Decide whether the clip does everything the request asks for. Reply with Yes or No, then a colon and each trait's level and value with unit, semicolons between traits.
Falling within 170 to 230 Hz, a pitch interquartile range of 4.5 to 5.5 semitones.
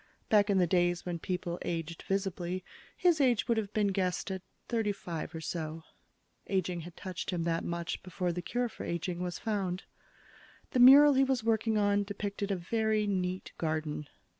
No: medium, 185 Hz; average, 3.6 semitones